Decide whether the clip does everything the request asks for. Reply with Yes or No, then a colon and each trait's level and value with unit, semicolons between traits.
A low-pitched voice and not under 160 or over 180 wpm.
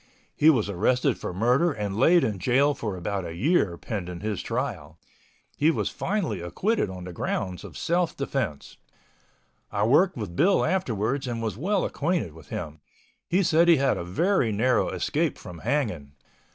Yes: low, 115 Hz; average, 170 wpm